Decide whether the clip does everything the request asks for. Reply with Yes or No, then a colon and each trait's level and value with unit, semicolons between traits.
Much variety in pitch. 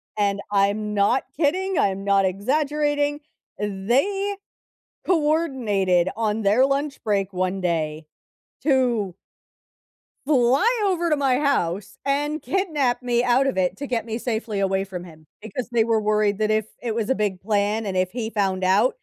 Yes: wide, 6.0 semitones